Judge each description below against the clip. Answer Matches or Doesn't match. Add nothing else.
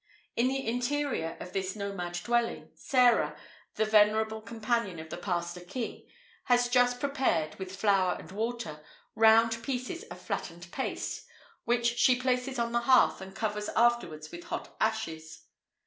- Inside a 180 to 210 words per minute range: Doesn't match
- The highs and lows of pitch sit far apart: Doesn't match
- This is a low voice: Doesn't match